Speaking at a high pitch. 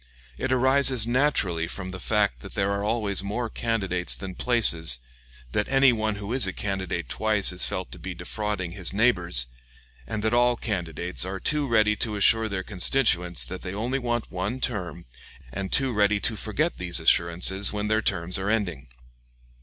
No: low, 100 Hz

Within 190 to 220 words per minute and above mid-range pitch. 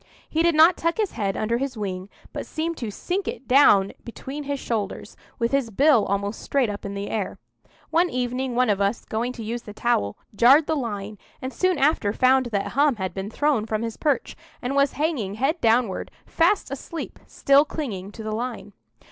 Yes: average, 200 wpm; high, 240 Hz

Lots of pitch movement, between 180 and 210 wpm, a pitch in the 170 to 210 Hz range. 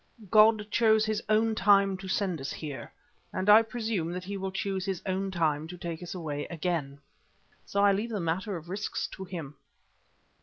No: average, 3.6 semitones; average, 190 wpm; high, 190 Hz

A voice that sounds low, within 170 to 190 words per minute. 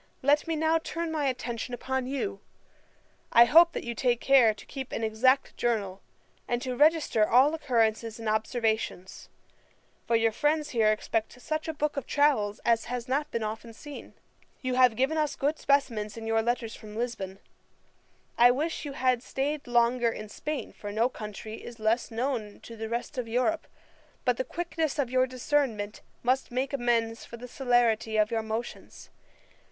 No: high, 245 Hz; average, 175 wpm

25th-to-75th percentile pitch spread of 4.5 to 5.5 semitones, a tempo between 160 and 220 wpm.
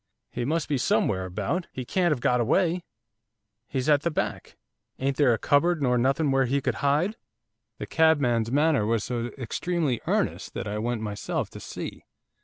Yes: average, 5.0 semitones; average, 180 wpm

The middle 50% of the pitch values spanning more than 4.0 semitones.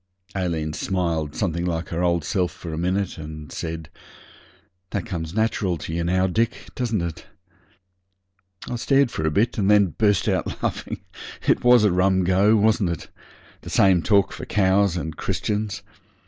No: average, 3.7 semitones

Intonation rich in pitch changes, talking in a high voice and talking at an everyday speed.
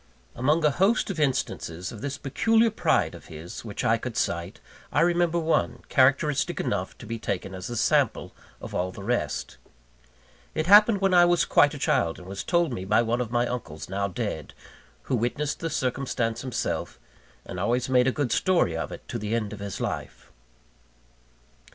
No: wide, 7.4 semitones; low, 125 Hz; average, 190 wpm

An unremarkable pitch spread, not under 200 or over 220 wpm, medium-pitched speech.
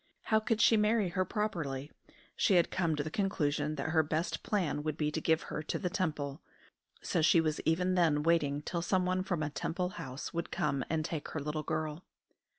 Yes: average, 3.4 semitones; fast, 205 wpm; medium, 160 Hz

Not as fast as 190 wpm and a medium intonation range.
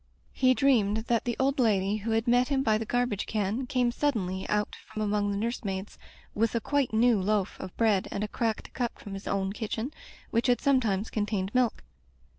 No: fast, 205 wpm; average, 3.2 semitones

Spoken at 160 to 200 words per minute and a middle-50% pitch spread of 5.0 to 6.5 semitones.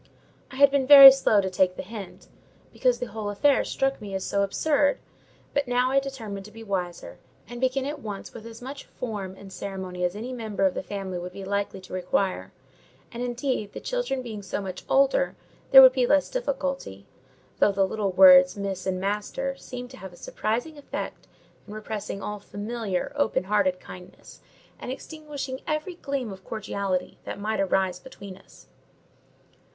Yes: average, 185 wpm; wide, 5.6 semitones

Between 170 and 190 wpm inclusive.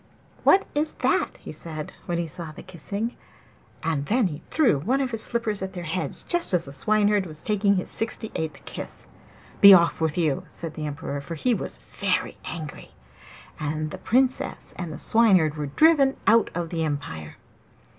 Yes: average, 185 wpm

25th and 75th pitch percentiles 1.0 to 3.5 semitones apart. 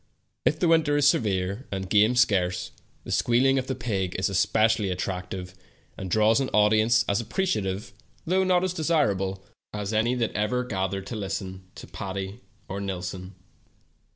No: average, 4.6 semitones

